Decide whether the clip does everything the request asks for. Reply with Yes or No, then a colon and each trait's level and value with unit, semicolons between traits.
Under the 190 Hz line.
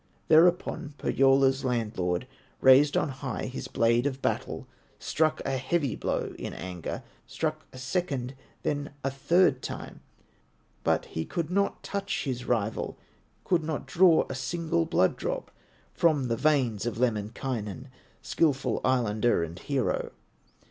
Yes: low, 135 Hz